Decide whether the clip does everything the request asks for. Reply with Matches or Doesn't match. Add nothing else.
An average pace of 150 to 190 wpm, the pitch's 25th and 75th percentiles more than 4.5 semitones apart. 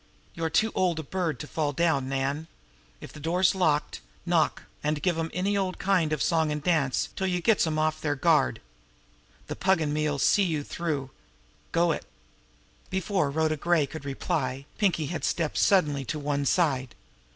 Doesn't match